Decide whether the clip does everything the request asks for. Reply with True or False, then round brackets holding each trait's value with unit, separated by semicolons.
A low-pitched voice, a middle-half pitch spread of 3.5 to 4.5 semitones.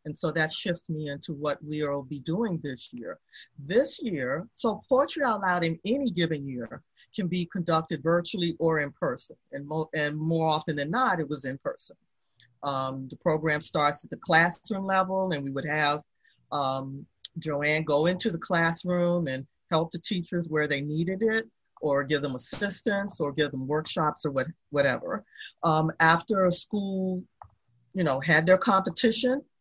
False (160 Hz; 4.1 semitones)